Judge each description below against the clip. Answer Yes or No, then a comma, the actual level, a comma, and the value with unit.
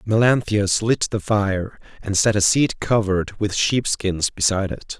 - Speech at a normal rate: Yes, average, 170 wpm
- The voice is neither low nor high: No, low, 105 Hz